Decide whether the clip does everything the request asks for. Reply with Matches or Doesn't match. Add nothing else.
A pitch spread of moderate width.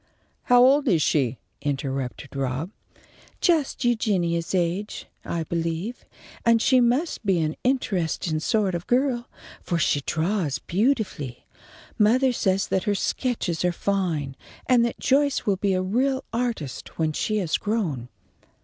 Doesn't match